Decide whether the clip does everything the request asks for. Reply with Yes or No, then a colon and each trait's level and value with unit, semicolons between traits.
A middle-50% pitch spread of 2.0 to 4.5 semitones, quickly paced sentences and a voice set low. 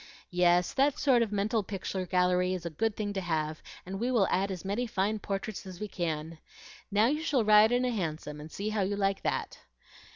No: average, 3.4 semitones; fast, 220 wpm; high, 195 Hz